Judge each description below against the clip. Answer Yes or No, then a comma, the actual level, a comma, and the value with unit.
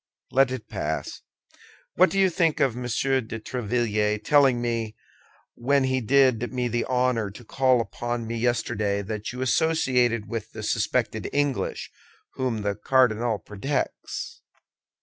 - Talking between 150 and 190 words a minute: No, average, 140 wpm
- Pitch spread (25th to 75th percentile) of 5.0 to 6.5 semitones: No, average, 3.0 semitones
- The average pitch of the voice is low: Yes, low, 120 Hz